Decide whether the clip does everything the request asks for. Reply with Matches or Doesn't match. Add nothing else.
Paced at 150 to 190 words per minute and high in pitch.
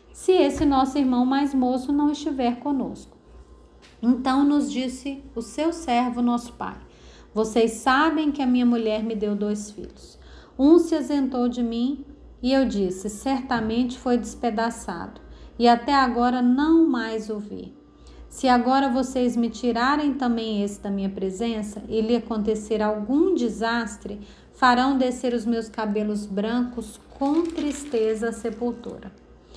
Doesn't match